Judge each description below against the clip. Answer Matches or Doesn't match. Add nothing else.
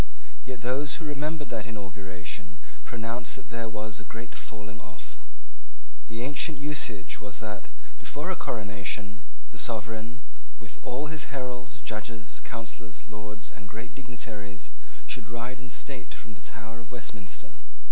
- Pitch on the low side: Matches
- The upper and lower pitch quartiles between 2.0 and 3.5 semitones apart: Matches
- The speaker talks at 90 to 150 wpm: Matches